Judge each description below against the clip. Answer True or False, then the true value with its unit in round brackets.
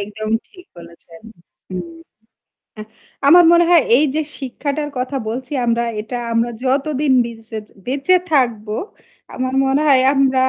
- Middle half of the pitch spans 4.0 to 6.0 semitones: True (4.3 semitones)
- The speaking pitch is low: False (260 Hz)